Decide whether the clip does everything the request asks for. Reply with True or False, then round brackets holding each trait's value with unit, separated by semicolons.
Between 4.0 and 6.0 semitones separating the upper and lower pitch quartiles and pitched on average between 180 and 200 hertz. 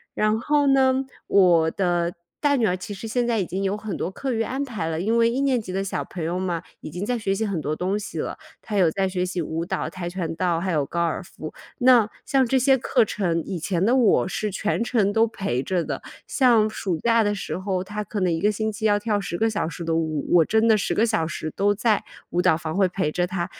True (4.3 semitones; 195 Hz)